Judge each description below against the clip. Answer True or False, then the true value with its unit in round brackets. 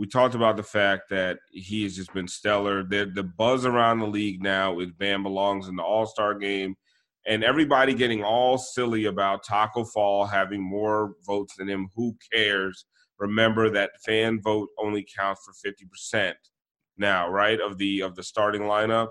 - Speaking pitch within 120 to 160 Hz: False (105 Hz)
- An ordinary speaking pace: True (180 wpm)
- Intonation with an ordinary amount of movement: False (2.1 semitones)